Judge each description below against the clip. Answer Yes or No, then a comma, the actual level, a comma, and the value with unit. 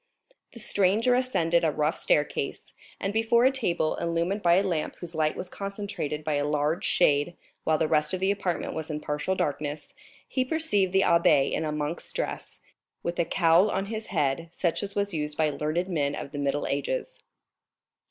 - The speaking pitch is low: No, medium, 170 Hz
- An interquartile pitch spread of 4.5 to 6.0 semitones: Yes, average, 4.8 semitones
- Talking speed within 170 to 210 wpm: Yes, average, 190 wpm